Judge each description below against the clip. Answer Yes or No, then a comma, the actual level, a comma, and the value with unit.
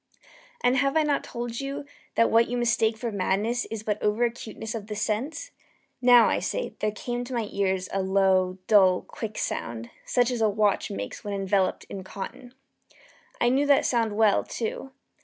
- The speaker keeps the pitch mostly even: No, average, 3.5 semitones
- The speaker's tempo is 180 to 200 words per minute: Yes, average, 185 wpm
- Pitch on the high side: Yes, high, 220 Hz